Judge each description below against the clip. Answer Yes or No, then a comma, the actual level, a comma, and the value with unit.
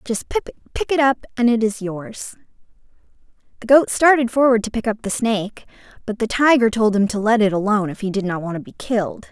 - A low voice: No, high, 220 Hz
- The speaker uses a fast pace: Yes, fast, 220 wpm